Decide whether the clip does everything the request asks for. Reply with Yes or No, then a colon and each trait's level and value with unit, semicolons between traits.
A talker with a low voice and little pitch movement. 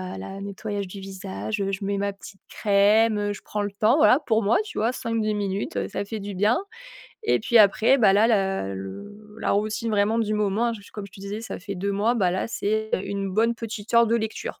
No: high, 205 Hz; narrow, 2.0 semitones